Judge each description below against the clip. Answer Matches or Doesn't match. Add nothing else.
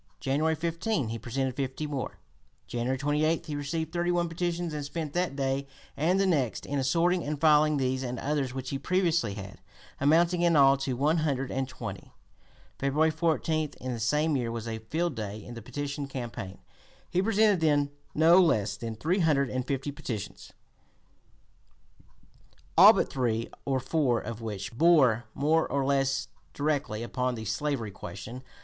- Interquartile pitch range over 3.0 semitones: Matches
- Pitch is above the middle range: Doesn't match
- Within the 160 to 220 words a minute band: Matches